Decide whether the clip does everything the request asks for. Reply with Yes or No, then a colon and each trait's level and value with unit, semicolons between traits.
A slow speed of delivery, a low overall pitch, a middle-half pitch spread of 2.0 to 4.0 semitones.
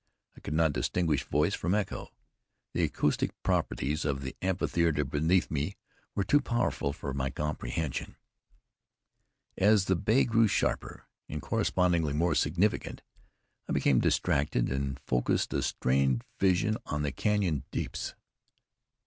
No: slow, 130 wpm; very low, 75 Hz; average, 5.1 semitones